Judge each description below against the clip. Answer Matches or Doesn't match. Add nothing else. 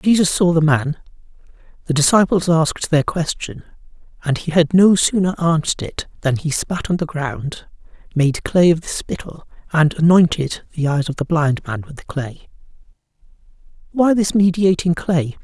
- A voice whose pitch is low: Doesn't match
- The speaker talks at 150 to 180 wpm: Matches